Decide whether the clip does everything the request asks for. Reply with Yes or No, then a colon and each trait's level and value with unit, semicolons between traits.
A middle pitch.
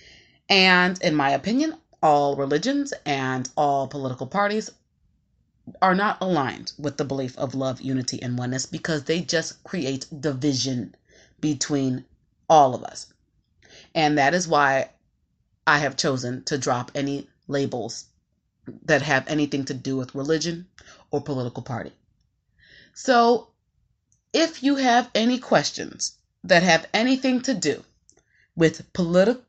Yes: medium, 150 Hz